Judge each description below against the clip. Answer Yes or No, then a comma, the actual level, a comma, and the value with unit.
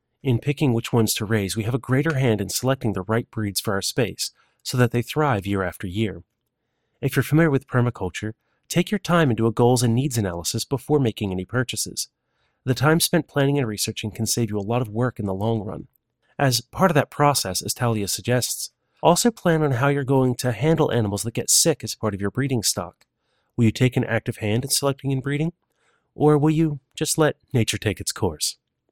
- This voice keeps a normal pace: No, fast, 220 wpm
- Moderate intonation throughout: Yes, average, 4.4 semitones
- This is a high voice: No, low, 120 Hz